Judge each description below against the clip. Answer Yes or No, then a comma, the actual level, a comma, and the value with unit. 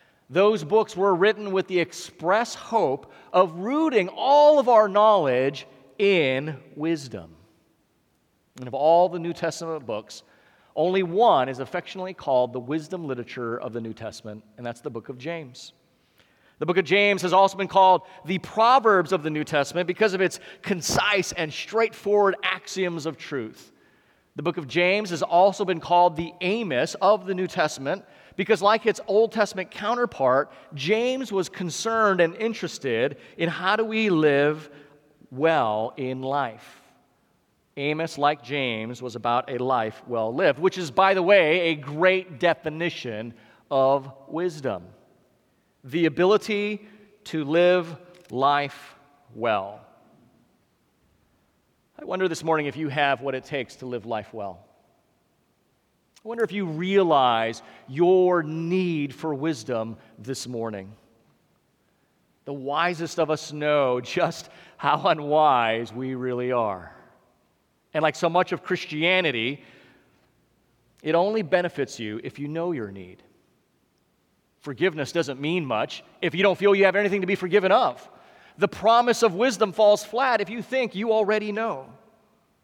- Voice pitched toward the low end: No, medium, 165 Hz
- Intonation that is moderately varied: No, wide, 6.2 semitones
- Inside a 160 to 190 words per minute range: No, average, 145 wpm